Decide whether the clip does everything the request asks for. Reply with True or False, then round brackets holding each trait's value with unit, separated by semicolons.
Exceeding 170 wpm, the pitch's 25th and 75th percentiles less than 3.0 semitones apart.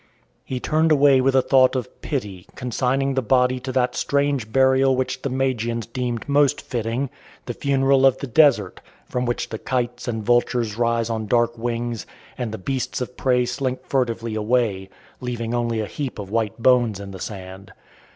True (180 wpm; 2.6 semitones)